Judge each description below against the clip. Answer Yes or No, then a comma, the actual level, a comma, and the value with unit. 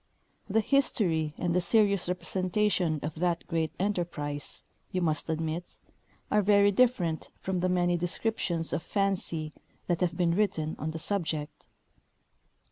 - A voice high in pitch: No, medium, 175 Hz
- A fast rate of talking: No, slow, 135 wpm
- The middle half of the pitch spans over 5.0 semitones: No, average, 3.5 semitones